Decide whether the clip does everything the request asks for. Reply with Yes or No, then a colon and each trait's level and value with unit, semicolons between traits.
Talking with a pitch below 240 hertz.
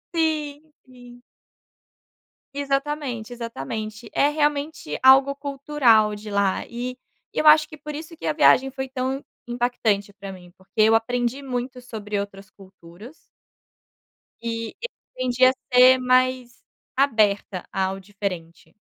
No: high, 245 Hz